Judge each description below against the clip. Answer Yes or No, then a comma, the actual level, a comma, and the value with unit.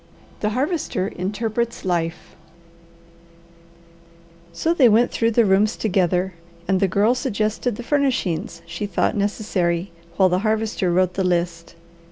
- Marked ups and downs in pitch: No, average, 3.8 semitones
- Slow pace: Yes, slow, 125 wpm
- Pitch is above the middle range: Yes, high, 200 Hz